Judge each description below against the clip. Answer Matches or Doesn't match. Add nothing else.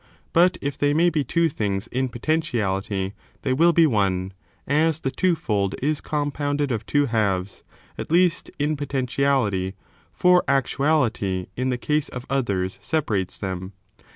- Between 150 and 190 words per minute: Matches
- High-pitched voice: Doesn't match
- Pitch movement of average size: Doesn't match